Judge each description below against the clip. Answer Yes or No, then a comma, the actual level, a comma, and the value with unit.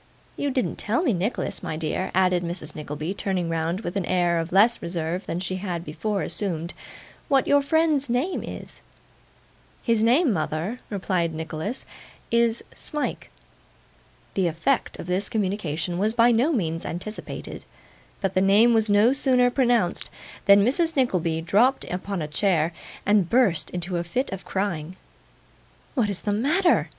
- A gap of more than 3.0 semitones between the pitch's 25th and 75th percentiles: Yes, wide, 5.6 semitones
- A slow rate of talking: No, average, 155 wpm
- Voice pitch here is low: No, high, 195 Hz